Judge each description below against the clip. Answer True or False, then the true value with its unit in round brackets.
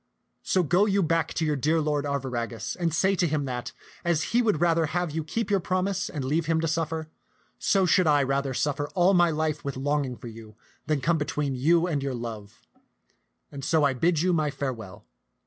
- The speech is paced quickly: True (210 wpm)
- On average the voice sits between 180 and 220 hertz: False (155 Hz)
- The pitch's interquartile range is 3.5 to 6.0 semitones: True (3.8 semitones)